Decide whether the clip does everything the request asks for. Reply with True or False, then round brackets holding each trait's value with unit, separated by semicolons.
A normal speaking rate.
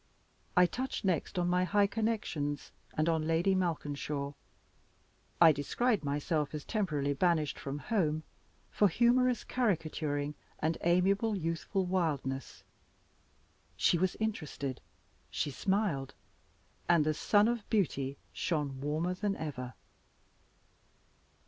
False (110 wpm)